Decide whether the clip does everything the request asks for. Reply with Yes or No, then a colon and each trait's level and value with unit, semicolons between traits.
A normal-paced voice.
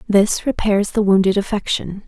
Yes: average, 145 wpm